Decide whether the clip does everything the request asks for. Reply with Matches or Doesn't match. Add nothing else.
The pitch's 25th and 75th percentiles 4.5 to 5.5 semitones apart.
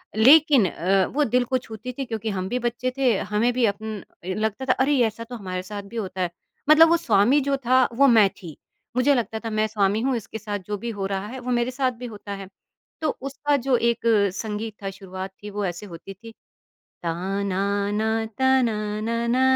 Doesn't match